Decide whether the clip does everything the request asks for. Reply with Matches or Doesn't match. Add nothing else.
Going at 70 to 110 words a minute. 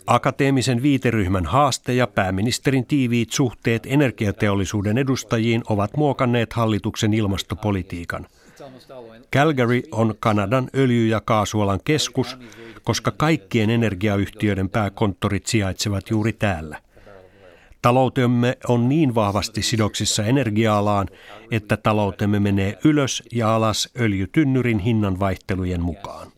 Matches